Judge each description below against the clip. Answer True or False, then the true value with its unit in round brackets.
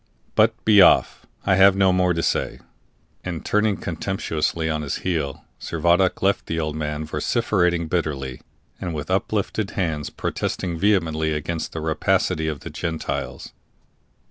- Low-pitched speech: True (85 Hz)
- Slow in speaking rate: False (145 wpm)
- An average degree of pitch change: True (3.6 semitones)